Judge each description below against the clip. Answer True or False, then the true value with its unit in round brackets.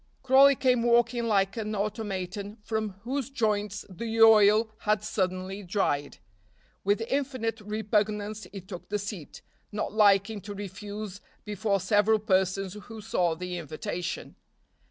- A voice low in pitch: False (210 Hz)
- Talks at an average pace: False (130 wpm)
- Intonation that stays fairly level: True (2.2 semitones)